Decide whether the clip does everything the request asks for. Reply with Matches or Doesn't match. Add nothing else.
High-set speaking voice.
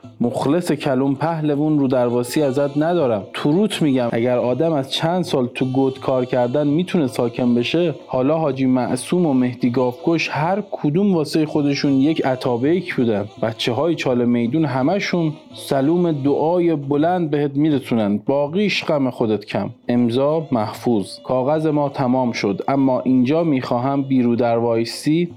Doesn't match